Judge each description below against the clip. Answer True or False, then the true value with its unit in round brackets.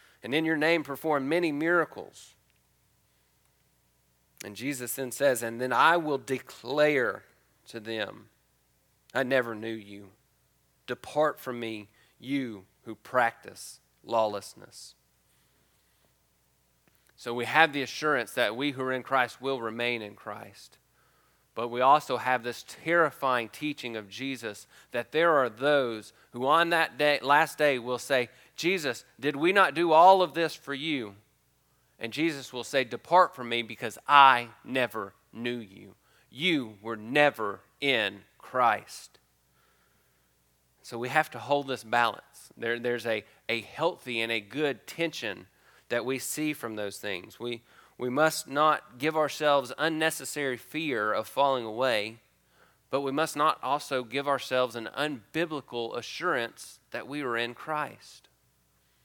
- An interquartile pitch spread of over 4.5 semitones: True (4.9 semitones)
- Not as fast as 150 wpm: True (140 wpm)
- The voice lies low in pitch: True (125 Hz)